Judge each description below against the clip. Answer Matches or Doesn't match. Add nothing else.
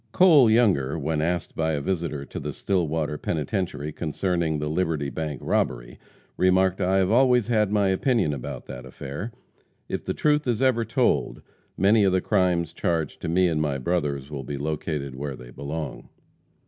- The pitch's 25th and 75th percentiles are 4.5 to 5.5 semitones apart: Matches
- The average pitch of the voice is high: Doesn't match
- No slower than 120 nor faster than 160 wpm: Doesn't match